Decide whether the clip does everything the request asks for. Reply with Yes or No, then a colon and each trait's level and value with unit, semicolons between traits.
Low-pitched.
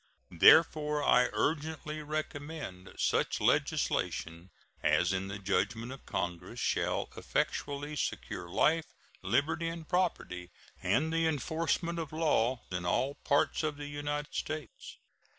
No: medium, 145 Hz